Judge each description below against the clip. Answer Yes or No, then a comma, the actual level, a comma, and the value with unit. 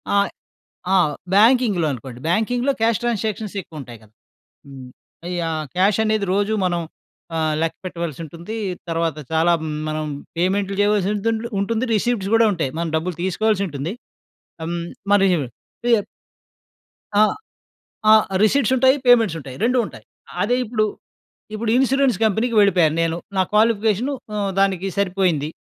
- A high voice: Yes, high, 195 Hz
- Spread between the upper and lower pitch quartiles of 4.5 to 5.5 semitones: Yes, average, 4.9 semitones